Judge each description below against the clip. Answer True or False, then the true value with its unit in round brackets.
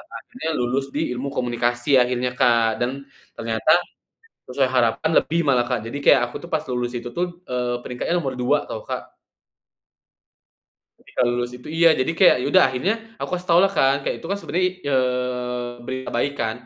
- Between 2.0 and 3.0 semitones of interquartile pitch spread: True (2.7 semitones)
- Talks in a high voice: False (125 Hz)